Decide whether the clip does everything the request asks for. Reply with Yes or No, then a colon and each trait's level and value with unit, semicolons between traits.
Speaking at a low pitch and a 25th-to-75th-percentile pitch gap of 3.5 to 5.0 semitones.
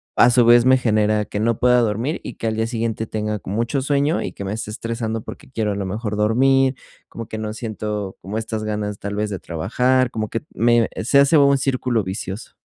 No: low, 110 Hz; average, 2.7 semitones